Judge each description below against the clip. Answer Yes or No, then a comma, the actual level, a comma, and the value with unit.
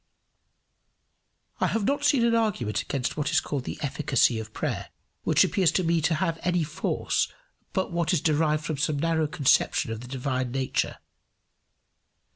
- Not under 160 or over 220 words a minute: Yes, average, 165 wpm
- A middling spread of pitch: Yes, average, 4.5 semitones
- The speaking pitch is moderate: Yes, medium, 155 Hz